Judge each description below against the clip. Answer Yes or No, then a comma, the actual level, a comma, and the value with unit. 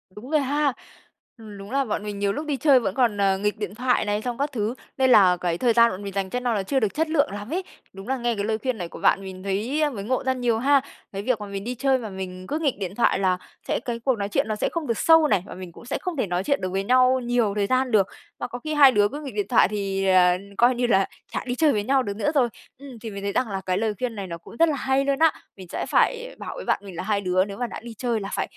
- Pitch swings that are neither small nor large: Yes, average, 4.8 semitones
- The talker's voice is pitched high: Yes, high, 225 Hz